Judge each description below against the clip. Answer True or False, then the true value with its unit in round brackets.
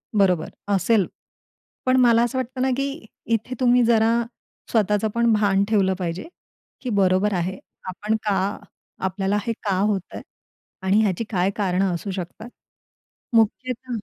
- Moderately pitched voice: False (210 Hz)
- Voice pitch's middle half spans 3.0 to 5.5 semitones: True (3.6 semitones)